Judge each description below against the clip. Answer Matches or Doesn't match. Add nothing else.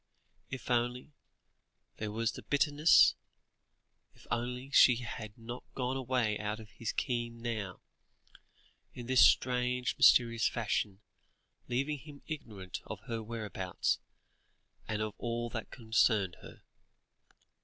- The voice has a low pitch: Matches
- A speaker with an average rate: Doesn't match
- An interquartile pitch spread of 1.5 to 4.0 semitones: Matches